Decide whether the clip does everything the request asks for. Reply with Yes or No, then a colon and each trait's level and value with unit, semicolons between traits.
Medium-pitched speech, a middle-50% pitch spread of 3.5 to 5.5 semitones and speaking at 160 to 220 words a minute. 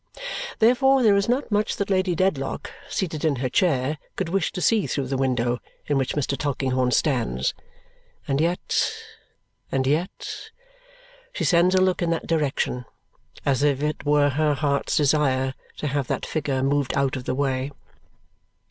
Yes: medium, 145 Hz; average, 5.0 semitones; average, 165 wpm